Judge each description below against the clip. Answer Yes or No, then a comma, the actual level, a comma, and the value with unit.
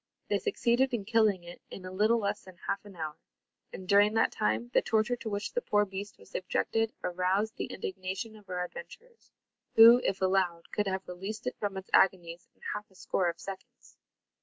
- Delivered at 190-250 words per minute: Yes, average, 200 wpm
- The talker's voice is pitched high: Yes, high, 200 Hz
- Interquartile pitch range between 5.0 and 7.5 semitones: No, average, 3.0 semitones